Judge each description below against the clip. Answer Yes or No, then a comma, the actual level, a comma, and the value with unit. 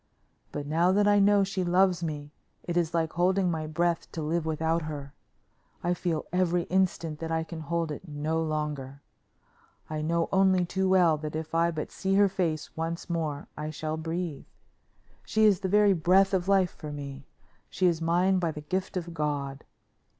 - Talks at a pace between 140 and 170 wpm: No, average, 185 wpm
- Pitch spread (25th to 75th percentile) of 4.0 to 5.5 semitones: No, average, 3.0 semitones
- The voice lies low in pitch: No, medium, 165 Hz